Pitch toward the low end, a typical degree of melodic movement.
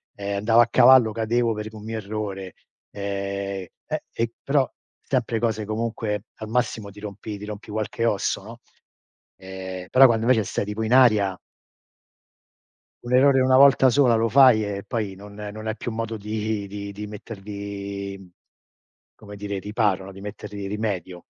No: low, 105 Hz; narrow, 2.3 semitones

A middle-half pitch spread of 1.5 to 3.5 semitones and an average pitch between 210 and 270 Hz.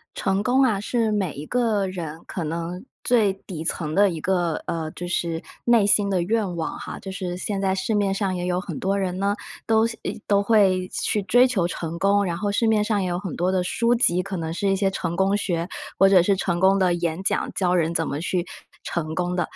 No: average, 2.8 semitones; high, 190 Hz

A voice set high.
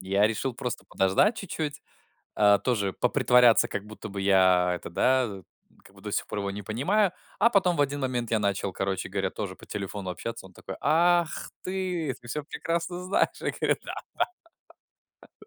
No: low, 115 Hz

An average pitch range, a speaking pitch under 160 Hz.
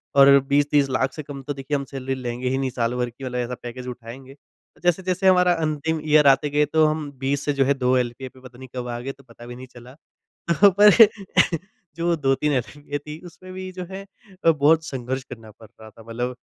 Yes: average, 3.3 semitones; low, 135 Hz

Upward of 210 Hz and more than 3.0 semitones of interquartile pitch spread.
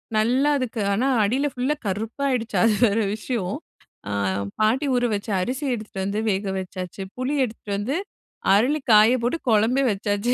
Yes: high, 225 Hz; average, 3.8 semitones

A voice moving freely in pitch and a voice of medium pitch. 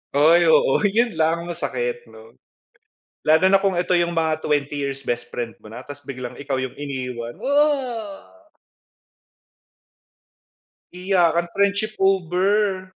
Yes: wide, 6.5 semitones; medium, 165 Hz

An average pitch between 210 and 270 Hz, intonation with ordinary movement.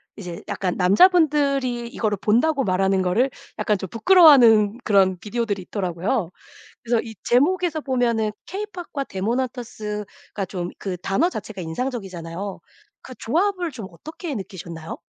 No: high, 225 Hz; wide, 6.3 semitones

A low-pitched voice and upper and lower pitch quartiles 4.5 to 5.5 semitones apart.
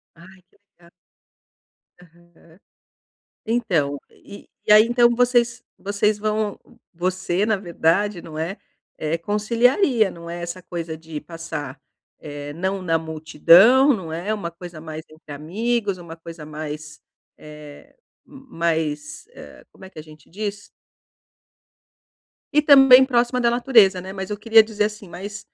No: medium, 185 Hz; average, 5.0 semitones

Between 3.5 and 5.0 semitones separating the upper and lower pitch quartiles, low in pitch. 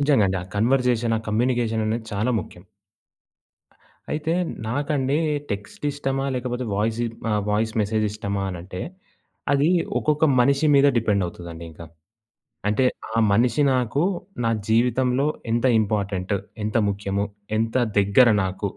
Yes: average, 4.2 semitones; low, 115 Hz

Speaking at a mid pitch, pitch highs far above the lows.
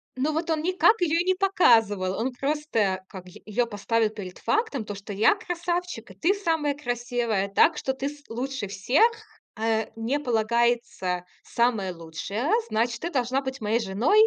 No: high, 240 Hz; wide, 5.9 semitones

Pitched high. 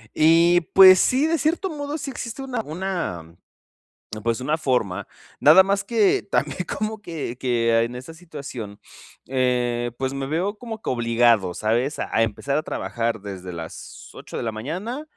No: medium, 140 Hz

